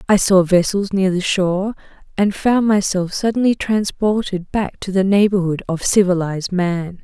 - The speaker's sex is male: No, female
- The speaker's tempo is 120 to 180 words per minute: Yes, average, 155 wpm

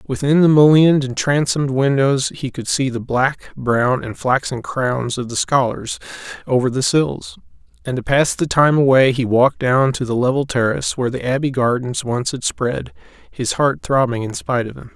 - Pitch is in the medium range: No, low, 130 Hz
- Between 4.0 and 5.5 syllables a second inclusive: Yes, 5.0 syllables/s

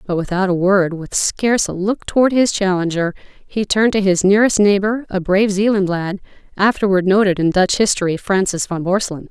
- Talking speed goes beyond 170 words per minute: Yes, average, 180 wpm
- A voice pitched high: Yes, high, 195 Hz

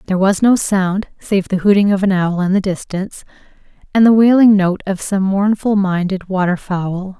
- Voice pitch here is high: Yes, high, 195 Hz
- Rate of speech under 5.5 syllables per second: Yes, 5.0 syllables/s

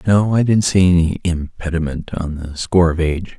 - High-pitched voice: No, very low, 85 Hz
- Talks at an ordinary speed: Yes, average, 195 wpm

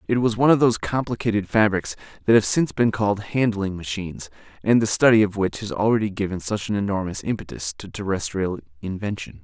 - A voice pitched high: No, low, 100 Hz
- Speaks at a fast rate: No, average, 185 wpm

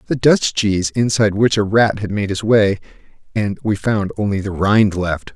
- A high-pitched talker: No, low, 105 Hz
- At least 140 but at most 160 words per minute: No, average, 200 wpm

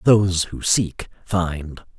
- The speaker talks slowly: Yes, slow, 120 wpm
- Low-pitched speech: Yes, very low, 90 Hz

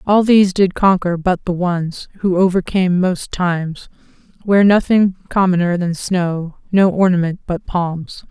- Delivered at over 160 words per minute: No, average, 145 wpm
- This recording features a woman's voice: Yes, female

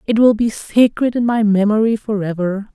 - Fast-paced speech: No, average, 175 wpm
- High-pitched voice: Yes, high, 215 Hz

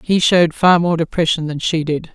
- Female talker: Yes, female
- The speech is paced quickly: Yes, fast, 225 wpm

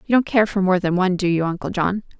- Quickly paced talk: Yes, fast, 300 wpm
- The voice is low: No, high, 190 Hz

